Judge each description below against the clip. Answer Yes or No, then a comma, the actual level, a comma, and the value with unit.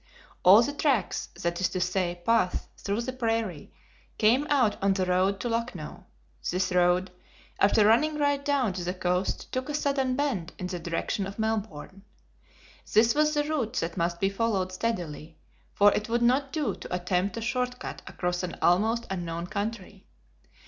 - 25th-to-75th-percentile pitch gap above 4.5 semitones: Yes, average, 4.9 semitones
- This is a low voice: No, high, 205 Hz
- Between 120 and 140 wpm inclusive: No, average, 175 wpm